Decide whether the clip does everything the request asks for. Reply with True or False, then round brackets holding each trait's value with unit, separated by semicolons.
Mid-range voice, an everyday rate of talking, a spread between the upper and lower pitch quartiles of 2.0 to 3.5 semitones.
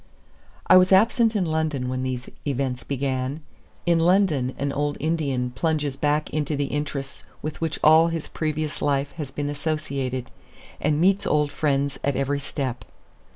True (145 Hz; 155 wpm; 2.5 semitones)